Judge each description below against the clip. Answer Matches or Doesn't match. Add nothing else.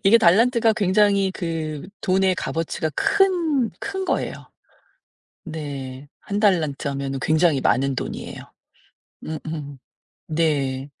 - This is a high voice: Doesn't match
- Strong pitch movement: Matches